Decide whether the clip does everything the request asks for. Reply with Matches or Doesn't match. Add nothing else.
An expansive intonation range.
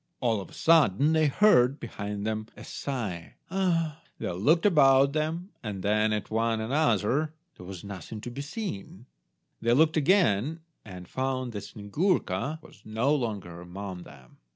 Matches